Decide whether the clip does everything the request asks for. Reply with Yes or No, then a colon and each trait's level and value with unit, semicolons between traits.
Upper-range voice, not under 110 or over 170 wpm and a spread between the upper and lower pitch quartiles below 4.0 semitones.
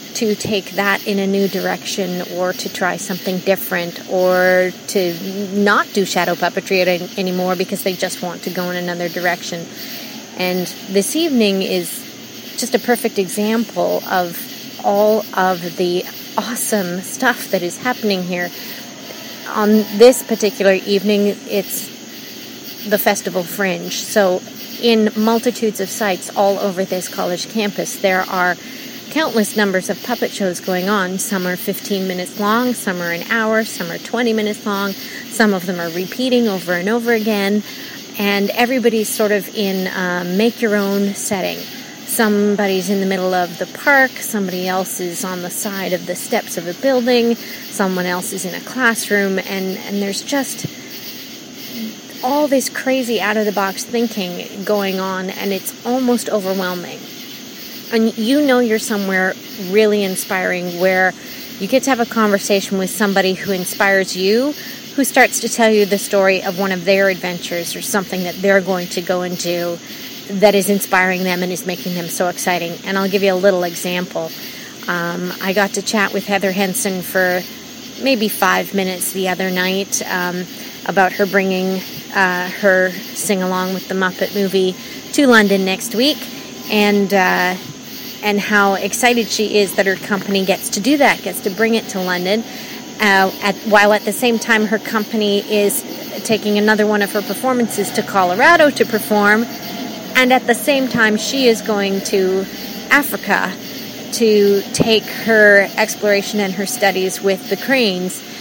Yes: high, 205 Hz; average, 160 wpm; average, 3.6 semitones